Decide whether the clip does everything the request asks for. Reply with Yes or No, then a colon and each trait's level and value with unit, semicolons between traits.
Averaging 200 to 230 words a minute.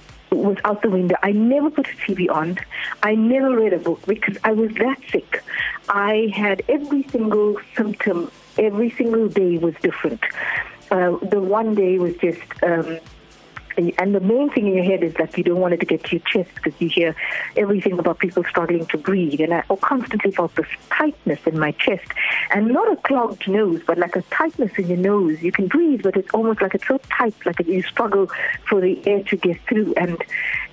Yes: fast, 205 wpm